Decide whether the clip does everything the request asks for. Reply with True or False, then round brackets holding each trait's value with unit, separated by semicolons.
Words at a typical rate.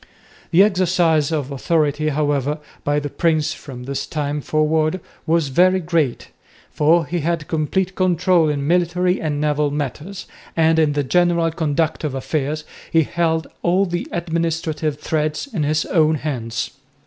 True (150 wpm)